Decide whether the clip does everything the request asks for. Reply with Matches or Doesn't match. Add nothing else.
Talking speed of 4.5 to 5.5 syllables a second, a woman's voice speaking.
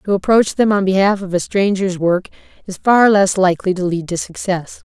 Matches